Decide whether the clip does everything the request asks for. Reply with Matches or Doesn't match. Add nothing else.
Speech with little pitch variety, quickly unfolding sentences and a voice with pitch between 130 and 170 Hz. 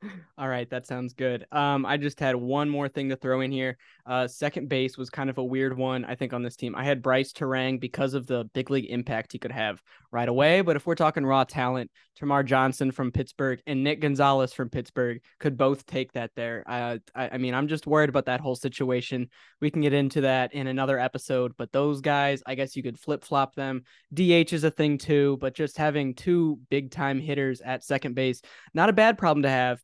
Matches